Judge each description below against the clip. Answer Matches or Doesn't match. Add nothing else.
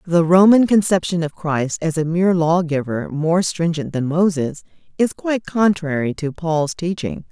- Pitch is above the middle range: Doesn't match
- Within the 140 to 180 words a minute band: Matches